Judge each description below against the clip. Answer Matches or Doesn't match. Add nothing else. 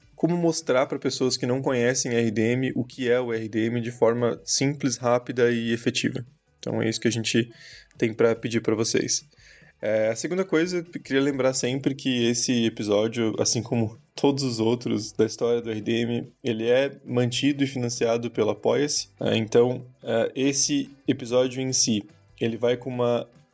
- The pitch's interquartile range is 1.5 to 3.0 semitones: Matches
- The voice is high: Doesn't match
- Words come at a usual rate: Matches